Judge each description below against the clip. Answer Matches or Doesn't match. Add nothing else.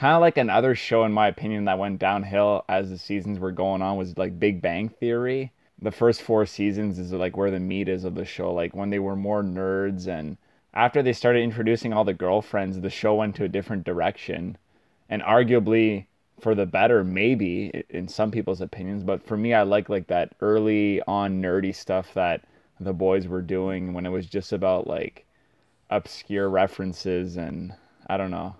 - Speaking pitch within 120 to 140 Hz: Doesn't match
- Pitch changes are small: Matches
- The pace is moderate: Matches